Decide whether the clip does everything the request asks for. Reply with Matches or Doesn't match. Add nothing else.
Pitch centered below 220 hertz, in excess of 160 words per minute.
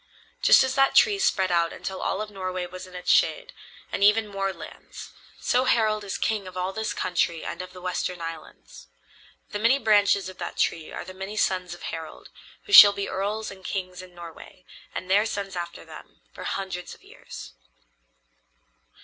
Matches